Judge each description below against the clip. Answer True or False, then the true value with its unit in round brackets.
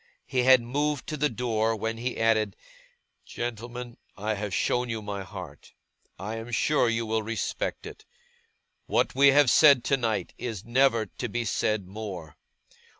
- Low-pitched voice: True (115 Hz)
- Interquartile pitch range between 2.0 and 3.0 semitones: True (2.5 semitones)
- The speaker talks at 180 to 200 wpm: False (155 wpm)